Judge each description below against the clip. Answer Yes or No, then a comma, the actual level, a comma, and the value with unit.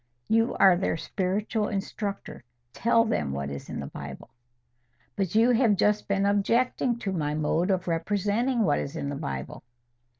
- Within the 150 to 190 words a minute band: Yes, average, 165 wpm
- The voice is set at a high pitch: Yes, high, 200 Hz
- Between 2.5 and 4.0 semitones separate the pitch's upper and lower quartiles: No, average, 5.2 semitones